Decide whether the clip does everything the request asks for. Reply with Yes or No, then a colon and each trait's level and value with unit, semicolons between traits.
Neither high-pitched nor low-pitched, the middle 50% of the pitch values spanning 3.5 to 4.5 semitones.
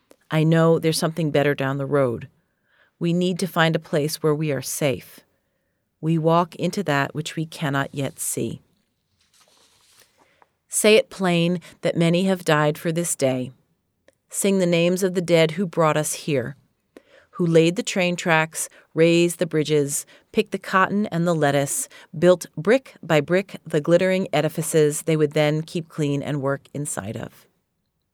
No: medium, 165 Hz; average, 2.8 semitones